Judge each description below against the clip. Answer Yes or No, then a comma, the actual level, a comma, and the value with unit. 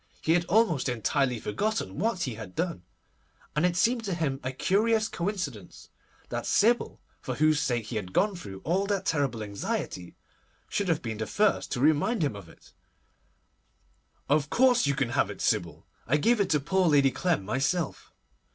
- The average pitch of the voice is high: No, medium, 155 Hz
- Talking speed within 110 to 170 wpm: No, average, 180 wpm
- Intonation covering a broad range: Yes, wide, 7.8 semitones